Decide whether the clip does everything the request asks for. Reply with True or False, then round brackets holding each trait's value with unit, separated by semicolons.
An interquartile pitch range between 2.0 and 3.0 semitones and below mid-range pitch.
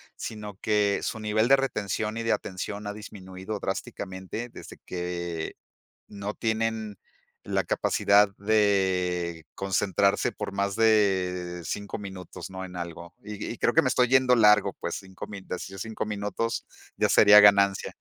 True (2.4 semitones; 100 Hz)